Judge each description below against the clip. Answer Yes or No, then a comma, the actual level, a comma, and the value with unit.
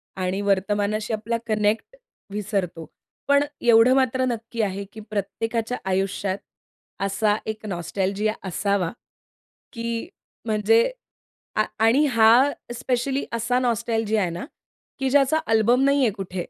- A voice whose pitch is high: Yes, high, 220 Hz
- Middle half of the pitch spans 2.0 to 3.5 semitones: Yes, average, 3.0 semitones